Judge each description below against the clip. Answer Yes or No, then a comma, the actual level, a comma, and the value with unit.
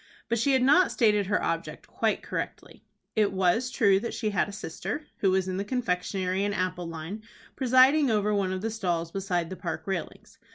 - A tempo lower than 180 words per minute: No, average, 200 wpm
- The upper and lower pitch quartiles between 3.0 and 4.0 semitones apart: Yes, average, 3.6 semitones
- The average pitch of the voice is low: No, high, 200 Hz